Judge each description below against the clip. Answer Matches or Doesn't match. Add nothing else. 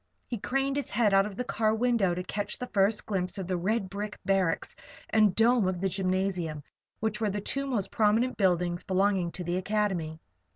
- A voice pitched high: Matches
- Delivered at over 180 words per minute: Matches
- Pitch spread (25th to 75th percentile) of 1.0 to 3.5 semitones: Matches